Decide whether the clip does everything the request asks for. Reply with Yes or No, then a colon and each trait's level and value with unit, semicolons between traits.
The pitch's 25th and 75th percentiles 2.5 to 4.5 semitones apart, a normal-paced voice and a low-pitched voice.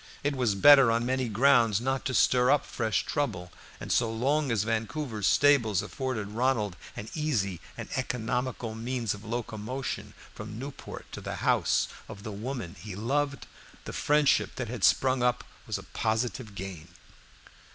Yes: average, 3.7 semitones; average, 160 wpm; low, 120 Hz